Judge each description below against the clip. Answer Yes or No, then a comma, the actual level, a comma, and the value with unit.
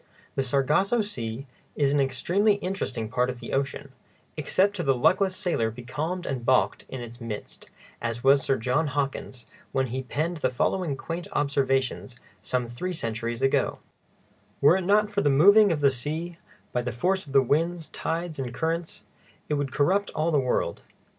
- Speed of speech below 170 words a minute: No, average, 175 wpm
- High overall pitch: No, medium, 140 Hz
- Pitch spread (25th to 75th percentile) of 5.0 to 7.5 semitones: Yes, wide, 5.4 semitones